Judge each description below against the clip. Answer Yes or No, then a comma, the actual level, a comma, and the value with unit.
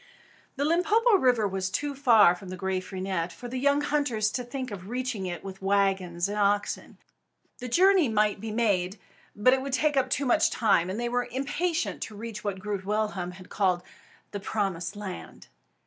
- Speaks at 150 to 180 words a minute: No, average, 190 wpm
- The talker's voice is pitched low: No, high, 210 Hz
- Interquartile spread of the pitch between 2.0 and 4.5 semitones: No, average, 5.2 semitones